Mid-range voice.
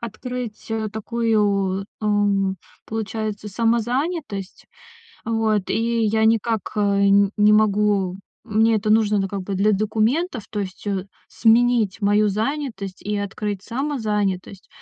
No: high, 210 Hz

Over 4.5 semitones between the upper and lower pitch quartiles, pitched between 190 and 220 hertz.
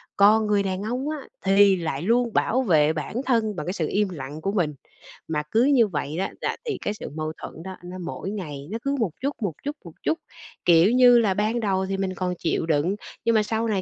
Yes: average, 5.2 semitones; high, 195 Hz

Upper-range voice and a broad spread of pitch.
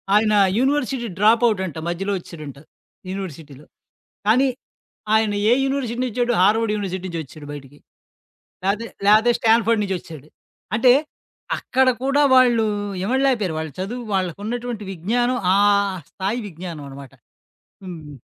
Yes: high, 210 Hz; wide, 5.8 semitones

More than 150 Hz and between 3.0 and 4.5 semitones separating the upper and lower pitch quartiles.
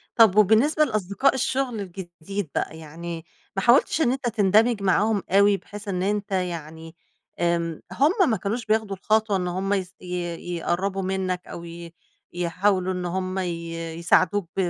Yes: high, 190 Hz; average, 3.5 semitones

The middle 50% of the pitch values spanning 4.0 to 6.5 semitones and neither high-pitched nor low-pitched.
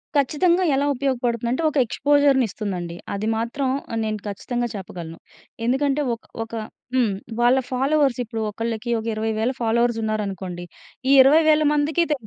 No: average, 4.4 semitones; high, 240 Hz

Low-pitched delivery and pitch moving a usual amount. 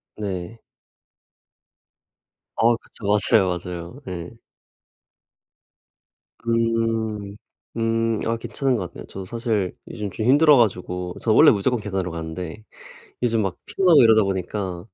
Yes: low, 105 Hz; average, 3.8 semitones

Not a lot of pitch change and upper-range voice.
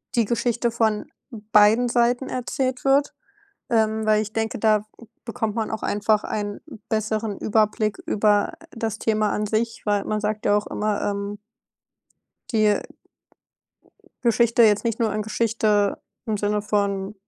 Yes: narrow, 1.6 semitones; high, 215 Hz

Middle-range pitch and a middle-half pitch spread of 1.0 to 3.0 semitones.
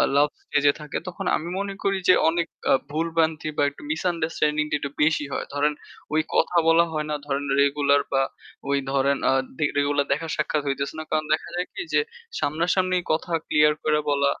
Yes: medium, 150 Hz; narrow, 2.5 semitones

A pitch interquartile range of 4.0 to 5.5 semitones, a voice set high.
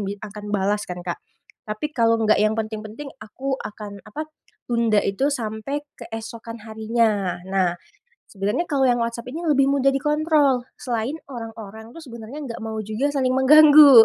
Yes: average, 4.3 semitones; high, 230 Hz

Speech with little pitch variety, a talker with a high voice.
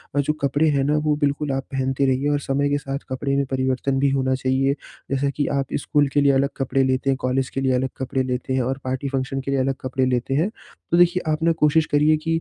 No: narrow, 1.5 semitones; low, 135 Hz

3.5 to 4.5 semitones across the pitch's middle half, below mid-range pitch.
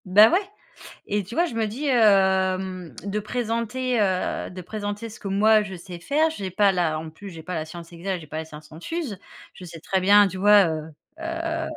No: average, 3.9 semitones; high, 195 Hz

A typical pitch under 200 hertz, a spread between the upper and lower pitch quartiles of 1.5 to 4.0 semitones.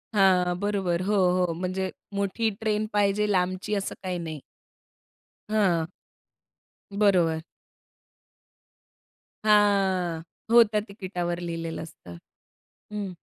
Yes: medium, 185 Hz; average, 2.9 semitones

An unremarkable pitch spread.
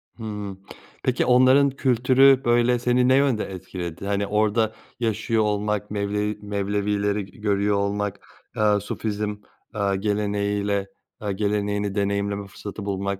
No: narrow, 1.6 semitones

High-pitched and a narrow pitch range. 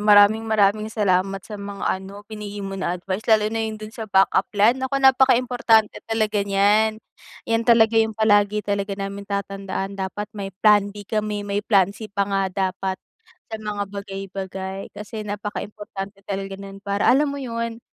Yes: high, 205 Hz; narrow, 1.8 semitones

